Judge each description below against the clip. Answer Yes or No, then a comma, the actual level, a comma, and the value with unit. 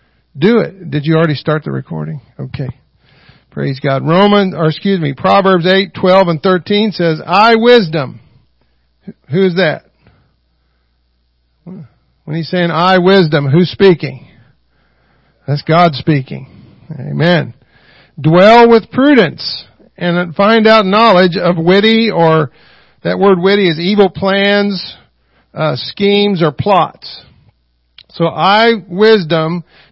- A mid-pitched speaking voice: Yes, medium, 170 Hz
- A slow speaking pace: Yes, slow, 120 wpm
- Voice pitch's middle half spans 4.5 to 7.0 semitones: Yes, average, 5.3 semitones